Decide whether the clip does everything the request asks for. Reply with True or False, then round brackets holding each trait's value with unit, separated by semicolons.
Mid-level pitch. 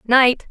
False (245 Hz)